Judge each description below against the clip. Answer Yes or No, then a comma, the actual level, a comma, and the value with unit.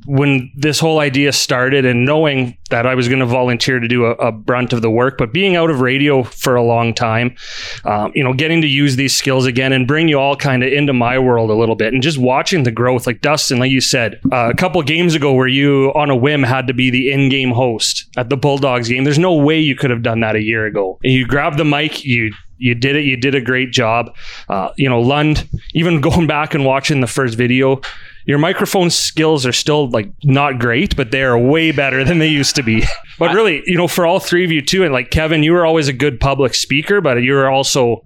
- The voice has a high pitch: No, low, 135 Hz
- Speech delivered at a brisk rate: Yes, fast, 250 wpm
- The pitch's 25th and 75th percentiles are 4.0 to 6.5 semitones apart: No, average, 3.2 semitones